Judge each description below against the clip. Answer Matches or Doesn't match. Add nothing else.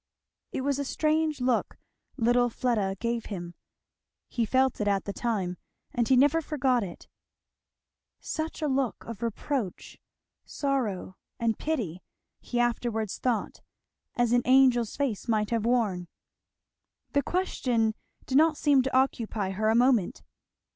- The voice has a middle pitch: Doesn't match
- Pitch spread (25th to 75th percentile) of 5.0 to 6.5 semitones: Doesn't match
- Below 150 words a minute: Matches